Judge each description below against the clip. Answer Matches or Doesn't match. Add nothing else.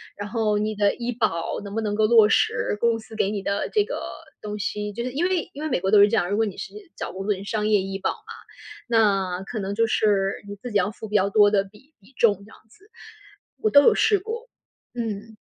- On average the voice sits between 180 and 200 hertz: Doesn't match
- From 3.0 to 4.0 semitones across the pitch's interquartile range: Doesn't match